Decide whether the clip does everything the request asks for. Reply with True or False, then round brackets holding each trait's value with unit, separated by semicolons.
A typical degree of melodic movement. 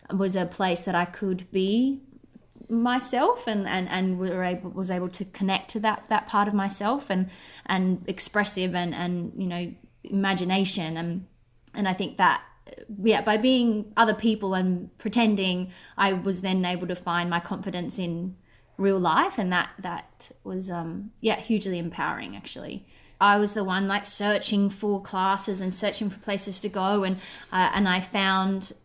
False (2.1 semitones)